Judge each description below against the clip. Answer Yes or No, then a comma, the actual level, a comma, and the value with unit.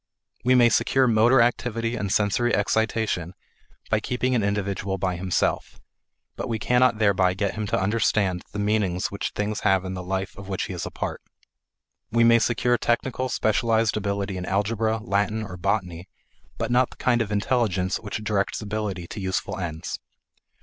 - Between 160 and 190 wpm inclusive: Yes, average, 170 wpm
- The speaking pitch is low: Yes, low, 105 Hz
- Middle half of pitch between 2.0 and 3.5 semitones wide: Yes, average, 3.2 semitones